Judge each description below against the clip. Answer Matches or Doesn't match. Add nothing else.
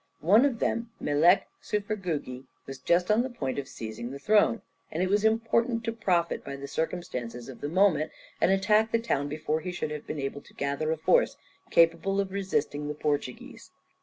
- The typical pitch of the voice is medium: Matches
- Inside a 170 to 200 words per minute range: Matches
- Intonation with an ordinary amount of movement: Doesn't match